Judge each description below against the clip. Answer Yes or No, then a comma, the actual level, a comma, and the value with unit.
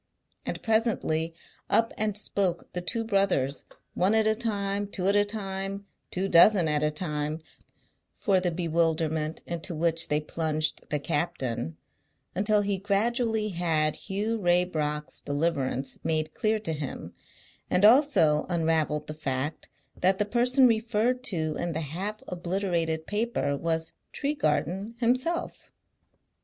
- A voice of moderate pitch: Yes, medium, 180 Hz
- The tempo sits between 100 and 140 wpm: Yes, slow, 135 wpm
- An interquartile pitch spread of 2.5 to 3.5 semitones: No, average, 5.1 semitones